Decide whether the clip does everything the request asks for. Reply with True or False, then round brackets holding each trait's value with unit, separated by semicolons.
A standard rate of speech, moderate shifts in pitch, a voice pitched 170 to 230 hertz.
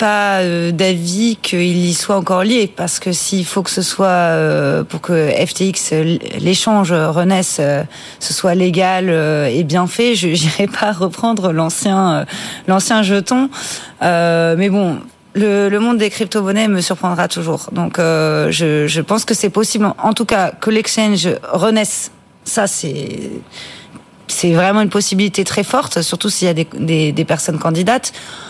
True (160 wpm; 3.5 semitones; 185 Hz)